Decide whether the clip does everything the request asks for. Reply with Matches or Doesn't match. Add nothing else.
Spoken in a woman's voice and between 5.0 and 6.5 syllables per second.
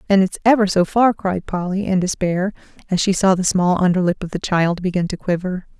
Matches